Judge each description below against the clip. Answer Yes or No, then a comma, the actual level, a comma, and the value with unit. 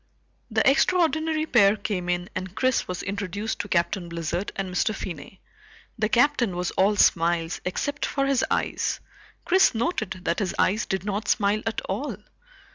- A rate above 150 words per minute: Yes, average, 160 wpm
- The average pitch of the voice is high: Yes, high, 200 Hz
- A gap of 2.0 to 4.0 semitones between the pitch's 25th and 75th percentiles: No, average, 5.1 semitones